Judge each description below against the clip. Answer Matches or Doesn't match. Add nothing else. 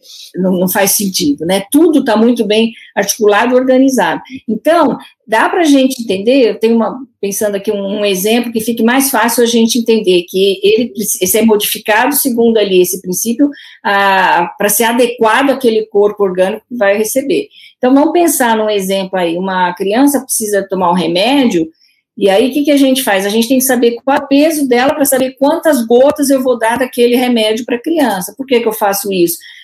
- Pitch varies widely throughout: Doesn't match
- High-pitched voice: Matches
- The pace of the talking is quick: Matches